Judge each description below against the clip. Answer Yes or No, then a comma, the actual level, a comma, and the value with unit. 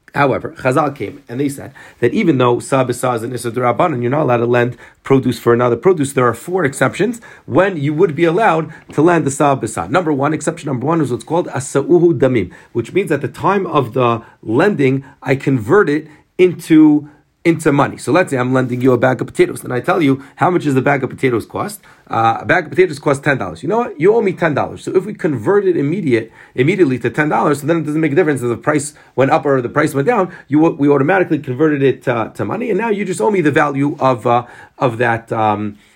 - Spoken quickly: Yes, fast, 240 wpm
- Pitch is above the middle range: No, medium, 140 Hz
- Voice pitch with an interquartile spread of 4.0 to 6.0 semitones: Yes, average, 4.6 semitones